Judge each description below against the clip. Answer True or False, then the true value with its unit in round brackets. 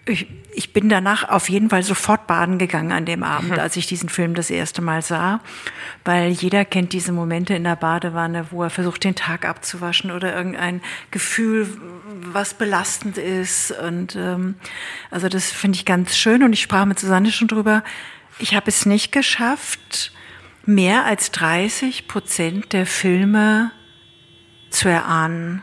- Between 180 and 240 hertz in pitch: True (185 Hz)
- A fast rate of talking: False (160 wpm)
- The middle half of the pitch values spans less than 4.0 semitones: True (2.9 semitones)